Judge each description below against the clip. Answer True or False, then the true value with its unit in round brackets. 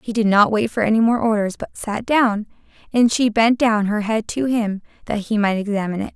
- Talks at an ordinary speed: False (235 wpm)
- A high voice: True (220 Hz)